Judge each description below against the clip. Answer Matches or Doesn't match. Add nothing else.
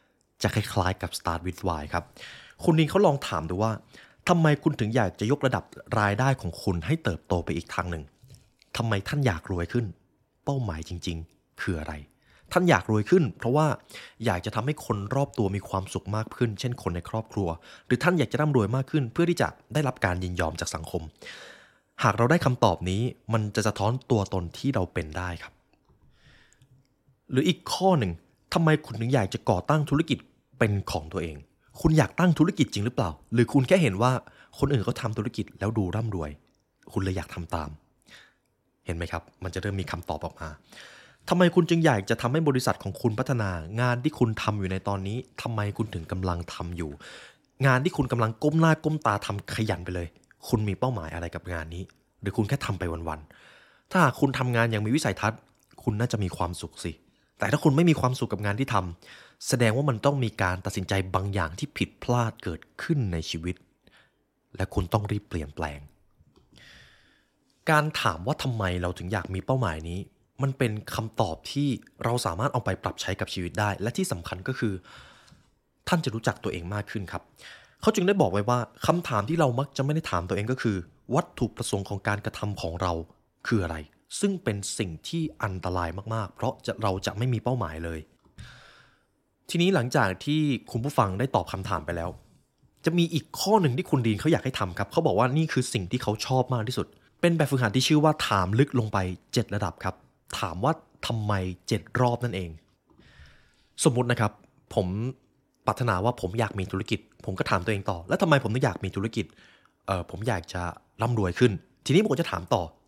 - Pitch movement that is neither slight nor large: Doesn't match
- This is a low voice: Matches